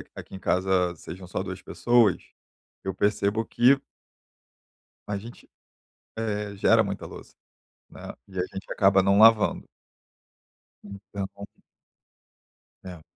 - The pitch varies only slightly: Yes, narrow, 2.2 semitones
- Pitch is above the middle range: No, low, 100 Hz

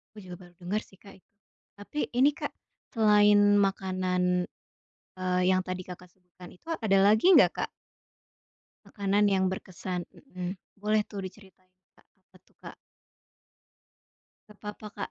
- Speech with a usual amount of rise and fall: No, narrow, 2.2 semitones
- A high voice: Yes, high, 195 Hz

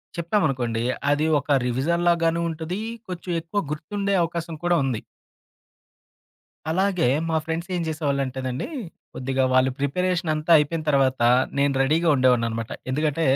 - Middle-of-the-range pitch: Yes, medium, 155 Hz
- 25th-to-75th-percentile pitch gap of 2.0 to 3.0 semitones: No, average, 4.3 semitones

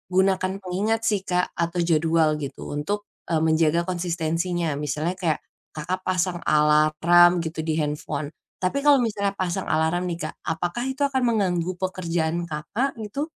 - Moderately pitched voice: Yes, medium, 175 Hz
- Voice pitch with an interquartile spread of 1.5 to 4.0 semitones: Yes, average, 2.8 semitones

